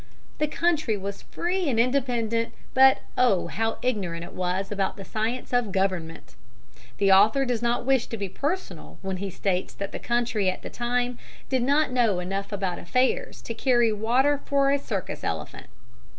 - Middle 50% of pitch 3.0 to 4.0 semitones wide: No, average, 4.7 semitones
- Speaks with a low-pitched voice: No, high, 230 Hz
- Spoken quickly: No, average, 175 wpm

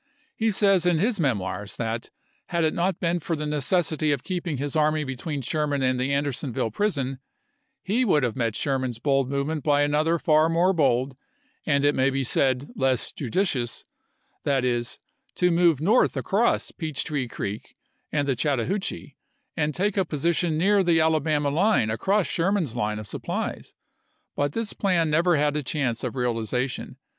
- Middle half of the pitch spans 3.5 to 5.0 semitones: Yes, average, 4.7 semitones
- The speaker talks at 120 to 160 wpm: No, average, 175 wpm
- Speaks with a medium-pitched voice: Yes, medium, 150 Hz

